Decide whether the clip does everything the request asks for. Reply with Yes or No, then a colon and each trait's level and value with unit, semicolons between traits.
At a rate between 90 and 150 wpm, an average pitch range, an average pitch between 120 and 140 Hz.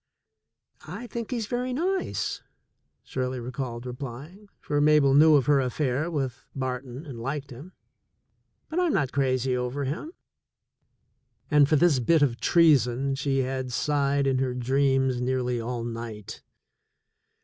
Yes: average, 140 wpm; average, 3.2 semitones; low, 135 Hz